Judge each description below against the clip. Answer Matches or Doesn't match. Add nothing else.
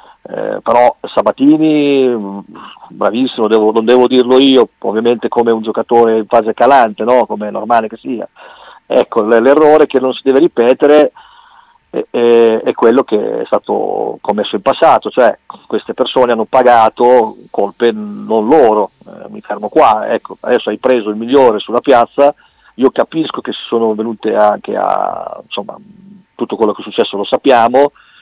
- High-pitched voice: Doesn't match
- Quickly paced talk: Doesn't match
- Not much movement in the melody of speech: Doesn't match